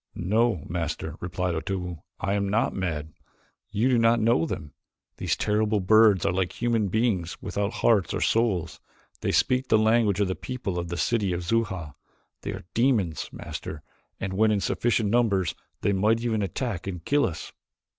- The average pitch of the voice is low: Yes, low, 100 Hz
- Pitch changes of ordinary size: Yes, average, 4.4 semitones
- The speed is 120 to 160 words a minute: No, average, 175 wpm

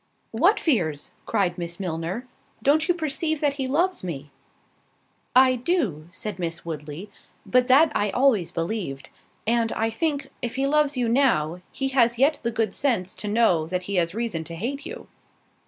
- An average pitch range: No, wide, 7.8 semitones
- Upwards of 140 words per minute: Yes, average, 170 wpm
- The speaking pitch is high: Yes, high, 230 Hz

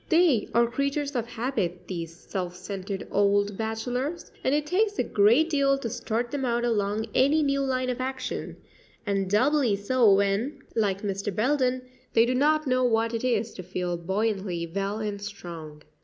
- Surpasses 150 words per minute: Yes, average, 170 wpm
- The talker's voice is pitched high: Yes, high, 225 Hz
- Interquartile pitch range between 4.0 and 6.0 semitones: Yes, average, 4.8 semitones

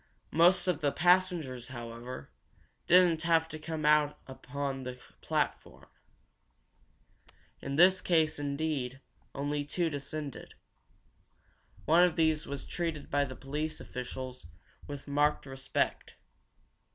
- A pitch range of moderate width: Yes, average, 3.2 semitones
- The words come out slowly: Yes, slow, 115 wpm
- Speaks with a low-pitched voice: No, medium, 150 Hz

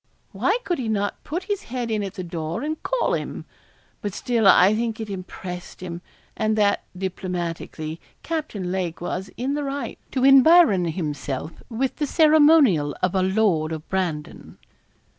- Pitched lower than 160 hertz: No, high, 200 Hz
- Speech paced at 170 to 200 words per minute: No, average, 160 wpm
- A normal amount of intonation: No, wide, 7.2 semitones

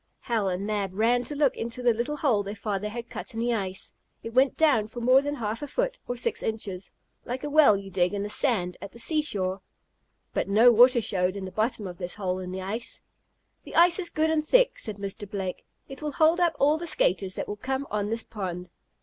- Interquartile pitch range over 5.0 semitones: Yes, wide, 5.5 semitones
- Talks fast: Yes, fast, 235 wpm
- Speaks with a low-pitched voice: No, high, 225 Hz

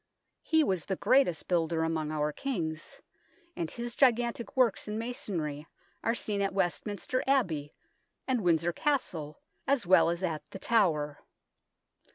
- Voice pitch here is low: No, medium, 185 Hz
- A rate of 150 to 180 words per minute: No, average, 140 wpm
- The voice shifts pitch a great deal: Yes, wide, 6.8 semitones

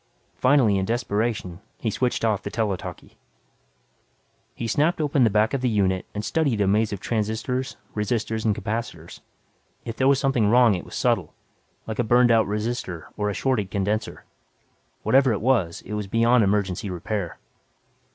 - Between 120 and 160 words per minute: No, average, 170 wpm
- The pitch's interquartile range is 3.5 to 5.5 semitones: No, average, 3.1 semitones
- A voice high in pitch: No, low, 110 Hz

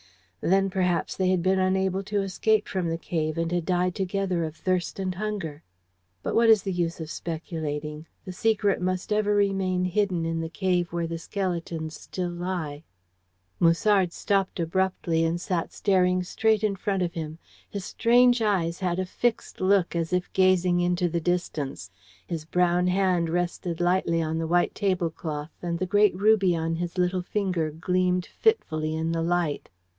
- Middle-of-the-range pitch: Yes, medium, 180 Hz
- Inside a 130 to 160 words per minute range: No, average, 170 wpm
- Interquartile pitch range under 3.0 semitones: Yes, narrow, 2.4 semitones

